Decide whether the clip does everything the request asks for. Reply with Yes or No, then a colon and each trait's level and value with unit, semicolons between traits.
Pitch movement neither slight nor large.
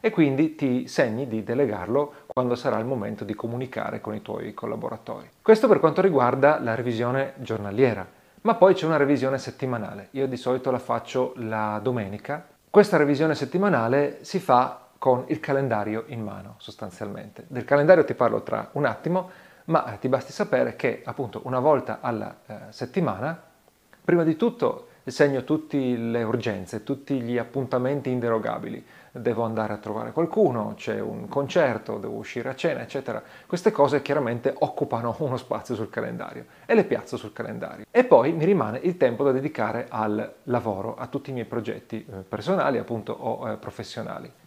Yes: average, 4.1 semitones